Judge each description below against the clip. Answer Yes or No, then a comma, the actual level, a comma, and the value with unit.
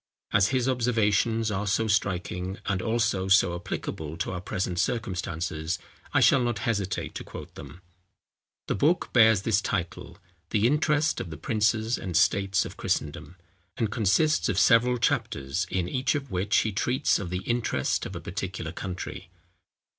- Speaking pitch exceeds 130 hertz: No, low, 100 Hz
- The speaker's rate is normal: Yes, average, 160 wpm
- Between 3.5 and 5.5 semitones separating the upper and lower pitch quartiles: Yes, average, 4.1 semitones